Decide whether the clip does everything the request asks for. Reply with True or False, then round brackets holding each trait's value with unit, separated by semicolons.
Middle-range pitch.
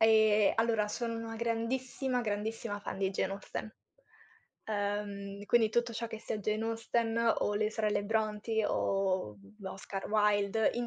False (215 Hz)